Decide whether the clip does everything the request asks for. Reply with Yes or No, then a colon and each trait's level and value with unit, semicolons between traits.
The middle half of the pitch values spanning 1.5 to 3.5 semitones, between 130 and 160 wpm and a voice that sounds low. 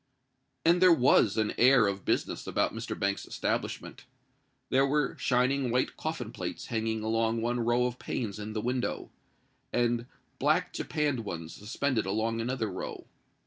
Yes: average, 2.8 semitones; average, 150 wpm; low, 120 Hz